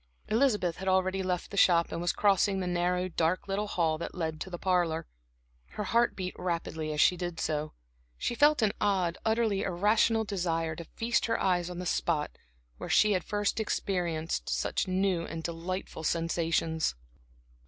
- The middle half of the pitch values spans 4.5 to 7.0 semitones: No, average, 3.1 semitones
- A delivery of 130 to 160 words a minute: No, average, 175 wpm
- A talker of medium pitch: Yes, medium, 180 Hz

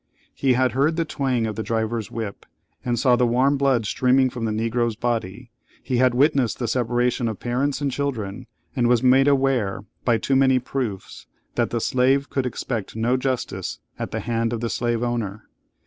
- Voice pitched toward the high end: No, low, 120 Hz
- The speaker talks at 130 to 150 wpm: No, average, 190 wpm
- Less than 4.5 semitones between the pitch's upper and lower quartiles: Yes, narrow, 2.4 semitones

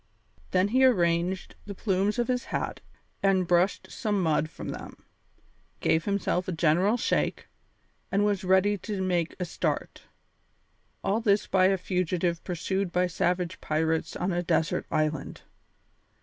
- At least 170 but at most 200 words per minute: No, average, 145 wpm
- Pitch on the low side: No, medium, 185 Hz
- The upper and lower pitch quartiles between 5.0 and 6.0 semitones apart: No, narrow, 2.6 semitones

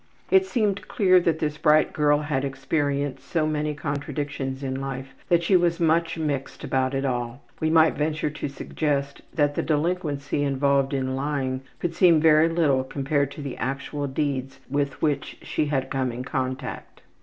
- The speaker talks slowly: No, average, 170 wpm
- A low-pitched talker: No, medium, 145 Hz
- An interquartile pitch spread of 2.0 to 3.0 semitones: Yes, narrow, 2.6 semitones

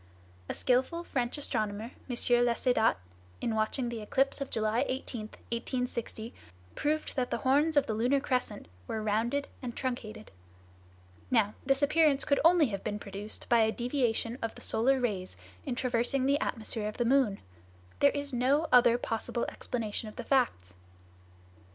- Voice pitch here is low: No, high, 245 Hz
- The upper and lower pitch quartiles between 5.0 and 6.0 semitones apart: No, average, 3.6 semitones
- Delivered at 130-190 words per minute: Yes, average, 155 wpm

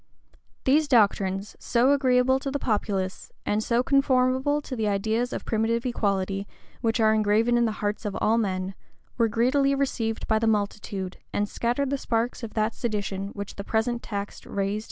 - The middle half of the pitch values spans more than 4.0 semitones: No, average, 3.5 semitones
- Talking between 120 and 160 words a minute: No, average, 190 wpm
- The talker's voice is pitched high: Yes, high, 225 Hz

